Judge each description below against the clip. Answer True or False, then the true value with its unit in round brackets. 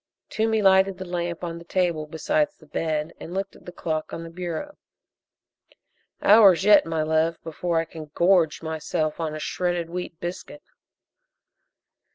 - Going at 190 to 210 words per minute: False (160 wpm)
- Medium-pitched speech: True (170 Hz)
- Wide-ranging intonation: False (2.8 semitones)